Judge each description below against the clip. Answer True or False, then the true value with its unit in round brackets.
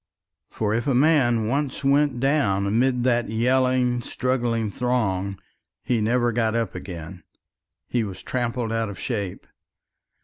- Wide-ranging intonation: False (2.9 semitones)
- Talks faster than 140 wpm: False (135 wpm)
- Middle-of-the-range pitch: False (120 Hz)